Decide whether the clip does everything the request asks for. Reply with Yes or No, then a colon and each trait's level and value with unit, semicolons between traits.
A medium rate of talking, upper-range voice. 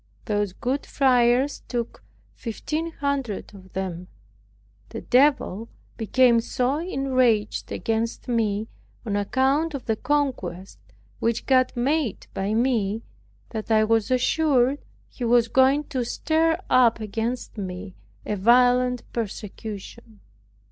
No: slow, 115 wpm; high, 240 Hz